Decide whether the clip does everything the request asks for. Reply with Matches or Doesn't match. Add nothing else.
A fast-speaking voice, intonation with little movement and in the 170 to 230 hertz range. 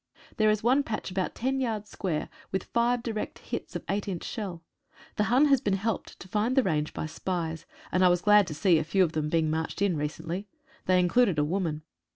Doesn't match